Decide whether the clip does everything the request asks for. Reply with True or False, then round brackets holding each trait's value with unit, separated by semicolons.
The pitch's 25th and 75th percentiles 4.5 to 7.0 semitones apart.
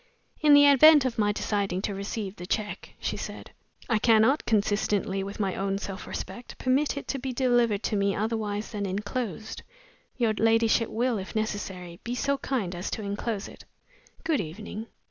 False (3.4 semitones)